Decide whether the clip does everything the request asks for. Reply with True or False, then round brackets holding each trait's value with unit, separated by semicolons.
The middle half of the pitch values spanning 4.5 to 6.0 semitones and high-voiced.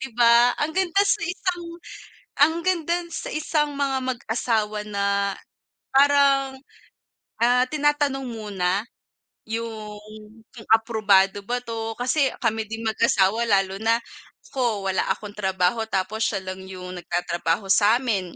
True (5.1 semitones; 225 Hz)